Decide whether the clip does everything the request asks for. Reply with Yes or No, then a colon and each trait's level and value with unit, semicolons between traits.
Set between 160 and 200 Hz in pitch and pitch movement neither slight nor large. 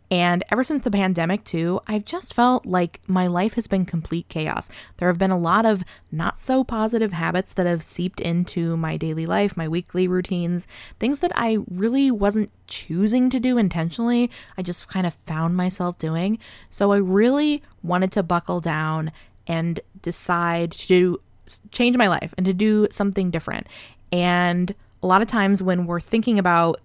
Yes: medium, 185 Hz; average, 3.7 semitones